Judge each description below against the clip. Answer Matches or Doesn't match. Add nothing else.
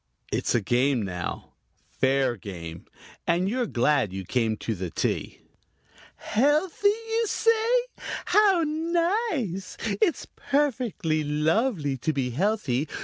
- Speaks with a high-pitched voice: Doesn't match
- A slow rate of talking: Matches